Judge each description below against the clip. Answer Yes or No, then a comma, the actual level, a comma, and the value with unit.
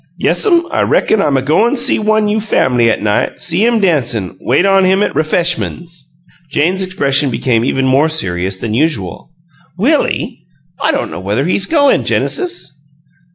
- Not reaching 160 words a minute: No, average, 165 wpm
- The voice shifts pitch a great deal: Yes, wide, 8.8 semitones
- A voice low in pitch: No, medium, 160 Hz